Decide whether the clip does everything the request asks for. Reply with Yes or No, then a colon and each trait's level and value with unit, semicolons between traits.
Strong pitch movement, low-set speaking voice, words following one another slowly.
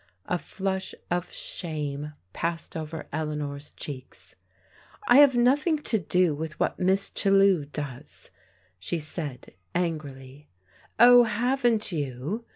No: wide, 5.8 semitones; medium, 165 Hz; slow, 120 wpm